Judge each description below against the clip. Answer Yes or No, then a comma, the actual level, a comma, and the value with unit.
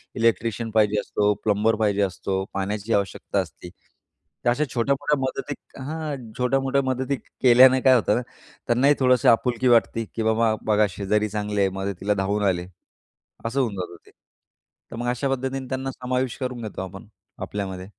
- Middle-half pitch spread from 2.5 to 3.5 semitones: No, average, 4.0 semitones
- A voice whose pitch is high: No, low, 115 Hz